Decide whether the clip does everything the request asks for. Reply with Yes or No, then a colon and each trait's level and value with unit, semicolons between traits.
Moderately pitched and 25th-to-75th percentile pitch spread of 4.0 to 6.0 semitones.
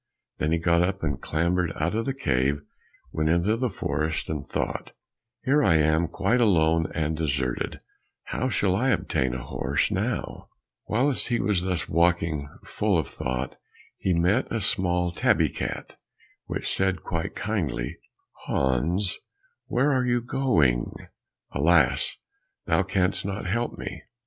No: very low, 85 Hz; average, 5.1 semitones